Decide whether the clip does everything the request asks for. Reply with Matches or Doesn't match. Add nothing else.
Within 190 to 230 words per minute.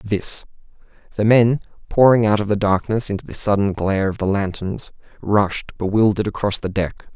Doesn't match